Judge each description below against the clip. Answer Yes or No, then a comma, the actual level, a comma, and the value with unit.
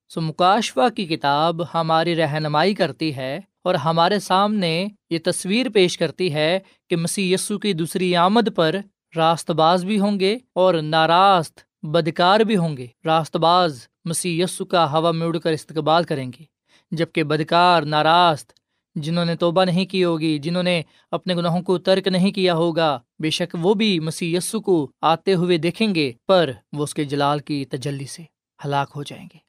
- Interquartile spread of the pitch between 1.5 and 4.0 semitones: Yes, narrow, 2.6 semitones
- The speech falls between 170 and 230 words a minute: Yes, average, 175 wpm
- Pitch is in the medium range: Yes, medium, 170 Hz